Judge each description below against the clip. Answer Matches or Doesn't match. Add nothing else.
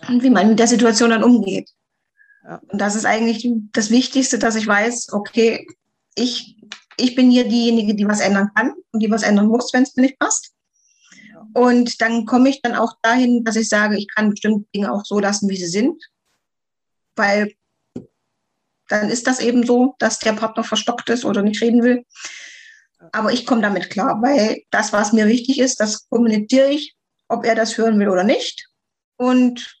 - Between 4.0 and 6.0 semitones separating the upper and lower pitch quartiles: Doesn't match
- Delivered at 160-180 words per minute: Doesn't match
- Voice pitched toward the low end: Doesn't match